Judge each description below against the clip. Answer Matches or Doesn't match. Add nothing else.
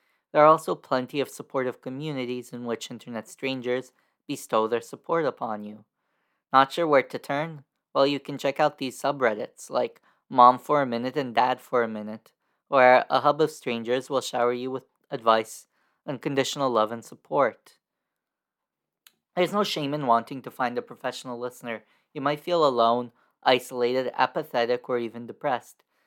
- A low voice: Matches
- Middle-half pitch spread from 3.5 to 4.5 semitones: Doesn't match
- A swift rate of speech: Doesn't match